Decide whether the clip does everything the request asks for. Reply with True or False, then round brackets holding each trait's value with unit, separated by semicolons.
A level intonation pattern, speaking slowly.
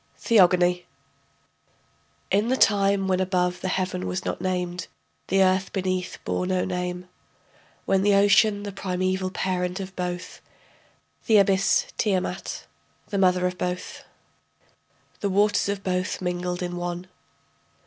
True (1.5 semitones; 130 wpm)